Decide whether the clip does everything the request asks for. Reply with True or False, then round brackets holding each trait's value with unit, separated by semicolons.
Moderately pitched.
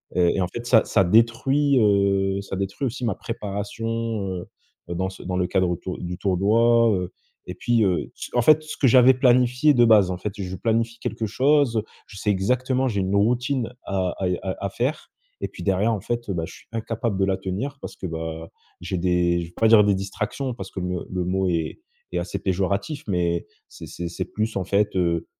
False (100 Hz)